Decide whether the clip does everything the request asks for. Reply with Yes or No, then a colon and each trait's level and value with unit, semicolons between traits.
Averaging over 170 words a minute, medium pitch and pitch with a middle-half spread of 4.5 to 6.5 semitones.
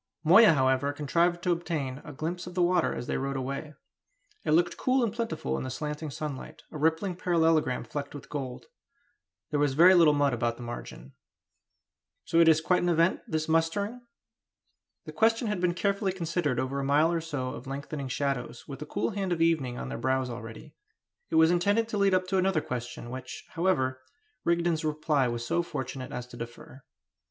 Yes: average, 195 wpm; medium, 155 Hz; average, 4.8 semitones